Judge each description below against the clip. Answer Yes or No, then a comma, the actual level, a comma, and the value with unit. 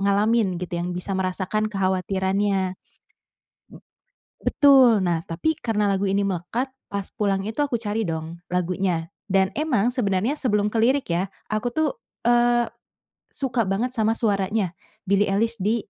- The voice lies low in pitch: No, high, 200 Hz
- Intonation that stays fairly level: No, average, 3.6 semitones